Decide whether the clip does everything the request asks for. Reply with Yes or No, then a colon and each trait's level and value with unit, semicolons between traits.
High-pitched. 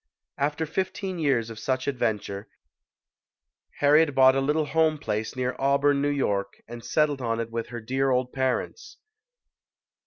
No: low, 135 Hz